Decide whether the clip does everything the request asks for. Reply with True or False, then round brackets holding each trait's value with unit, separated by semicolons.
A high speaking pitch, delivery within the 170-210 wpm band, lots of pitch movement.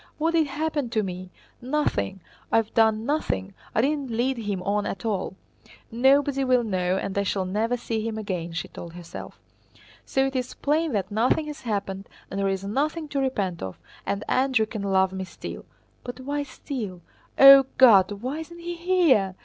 True (230 Hz; 185 wpm; 6.0 semitones)